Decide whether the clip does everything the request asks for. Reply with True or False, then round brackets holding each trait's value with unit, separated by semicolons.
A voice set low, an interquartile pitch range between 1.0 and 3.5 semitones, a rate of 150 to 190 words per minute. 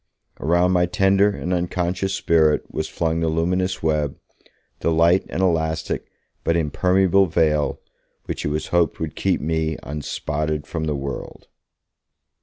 False (80 Hz; 2.8 semitones; 140 wpm)